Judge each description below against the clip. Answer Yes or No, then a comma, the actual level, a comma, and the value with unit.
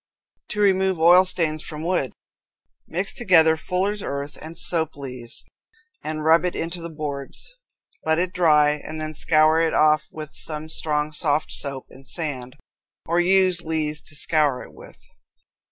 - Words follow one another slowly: No, average, 155 wpm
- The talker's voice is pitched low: No, medium, 160 Hz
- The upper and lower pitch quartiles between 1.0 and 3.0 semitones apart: Yes, narrow, 2.5 semitones